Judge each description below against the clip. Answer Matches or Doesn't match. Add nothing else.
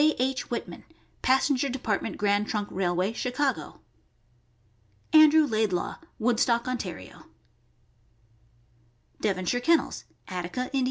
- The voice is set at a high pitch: Matches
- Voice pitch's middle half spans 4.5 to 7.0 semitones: Matches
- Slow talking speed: Matches